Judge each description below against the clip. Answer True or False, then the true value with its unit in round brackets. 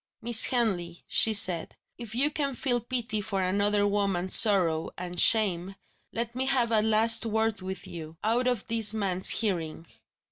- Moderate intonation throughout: True (3.7 semitones)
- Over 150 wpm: True (165 wpm)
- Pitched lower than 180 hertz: False (215 Hz)